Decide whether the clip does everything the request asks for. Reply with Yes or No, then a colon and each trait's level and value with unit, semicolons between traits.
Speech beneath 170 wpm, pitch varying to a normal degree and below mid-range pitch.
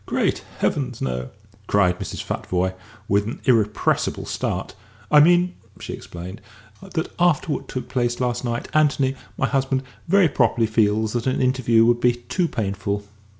Yes: average, 150 wpm; average, 4.7 semitones; low, 120 Hz